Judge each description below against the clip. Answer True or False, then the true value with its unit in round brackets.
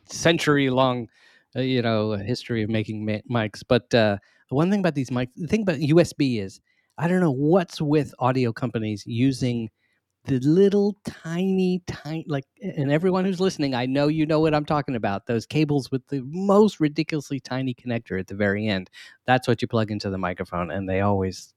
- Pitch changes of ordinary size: False (5.9 semitones)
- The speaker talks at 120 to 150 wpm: False (190 wpm)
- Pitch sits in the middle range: False (130 Hz)